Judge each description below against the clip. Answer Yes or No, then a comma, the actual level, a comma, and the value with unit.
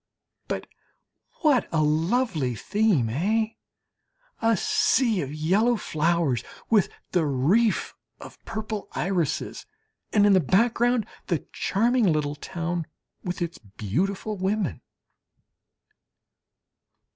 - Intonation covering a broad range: Yes, wide, 6.0 semitones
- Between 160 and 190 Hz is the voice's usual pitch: Yes, medium, 185 Hz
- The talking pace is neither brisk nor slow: No, slow, 100 wpm